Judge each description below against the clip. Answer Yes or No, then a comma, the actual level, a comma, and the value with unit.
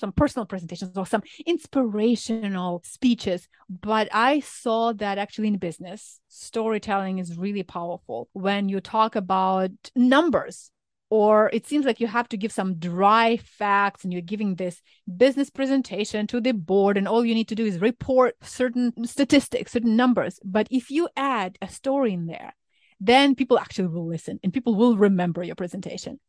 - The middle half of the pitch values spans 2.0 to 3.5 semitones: No, average, 4.4 semitones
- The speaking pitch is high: Yes, high, 215 Hz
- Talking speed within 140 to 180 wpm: Yes, average, 170 wpm